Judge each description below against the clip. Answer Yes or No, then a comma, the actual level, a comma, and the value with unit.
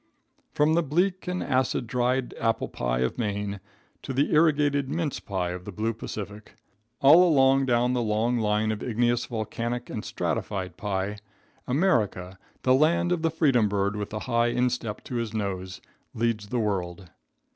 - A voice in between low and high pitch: No, low, 115 Hz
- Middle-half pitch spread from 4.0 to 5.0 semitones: Yes, average, 4.5 semitones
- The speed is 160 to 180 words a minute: Yes, average, 165 wpm